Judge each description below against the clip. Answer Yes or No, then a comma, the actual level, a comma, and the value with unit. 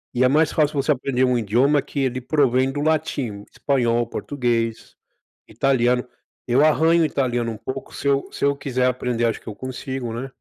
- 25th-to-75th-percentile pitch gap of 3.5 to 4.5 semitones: No, average, 2.8 semitones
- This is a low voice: Yes, low, 130 Hz